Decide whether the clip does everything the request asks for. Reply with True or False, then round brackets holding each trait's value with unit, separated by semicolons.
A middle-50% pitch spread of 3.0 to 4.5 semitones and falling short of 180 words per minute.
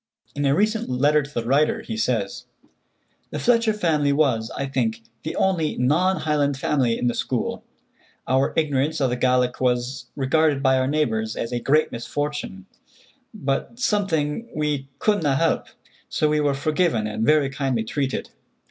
True (3.5 semitones; 160 wpm)